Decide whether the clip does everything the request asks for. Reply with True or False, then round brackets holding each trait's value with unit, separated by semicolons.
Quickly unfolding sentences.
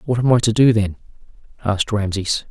False (190 wpm)